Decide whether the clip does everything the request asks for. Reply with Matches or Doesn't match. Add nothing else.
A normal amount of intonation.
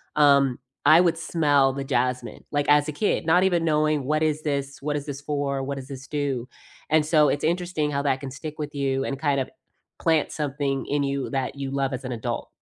Doesn't match